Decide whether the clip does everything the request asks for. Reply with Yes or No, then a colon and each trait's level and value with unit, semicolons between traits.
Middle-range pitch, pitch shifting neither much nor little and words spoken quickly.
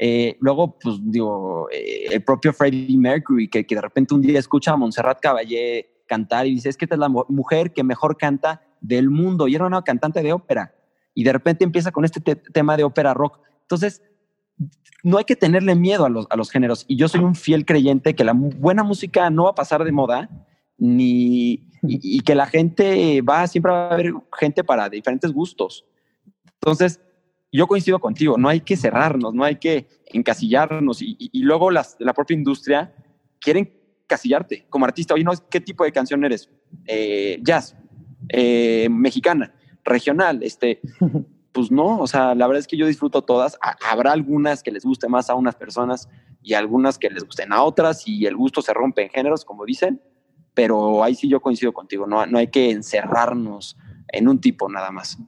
No: medium, 145 Hz; wide, 5.9 semitones; fast, 195 wpm